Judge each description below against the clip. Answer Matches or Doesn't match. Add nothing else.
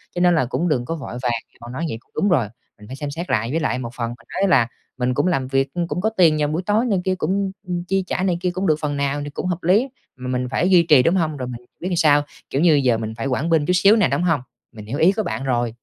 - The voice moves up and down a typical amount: Doesn't match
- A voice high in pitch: Doesn't match